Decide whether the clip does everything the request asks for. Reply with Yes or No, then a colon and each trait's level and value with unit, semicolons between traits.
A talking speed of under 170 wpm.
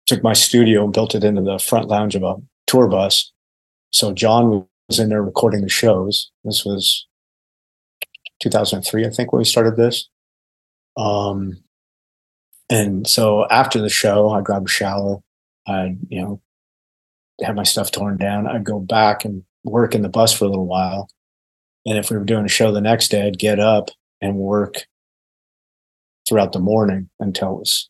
No: average, 175 wpm